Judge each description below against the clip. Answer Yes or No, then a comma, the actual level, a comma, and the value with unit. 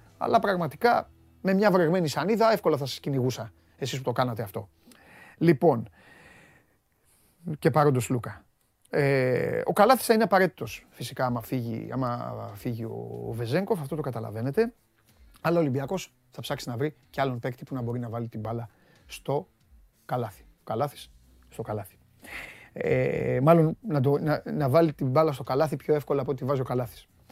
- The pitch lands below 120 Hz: No, low, 135 Hz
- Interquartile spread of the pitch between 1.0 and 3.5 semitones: No, wide, 5.4 semitones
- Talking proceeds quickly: No, average, 155 wpm